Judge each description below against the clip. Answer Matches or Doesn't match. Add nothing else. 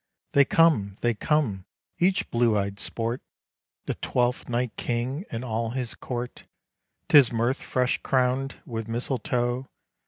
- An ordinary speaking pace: Doesn't match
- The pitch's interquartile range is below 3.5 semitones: Matches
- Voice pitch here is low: Matches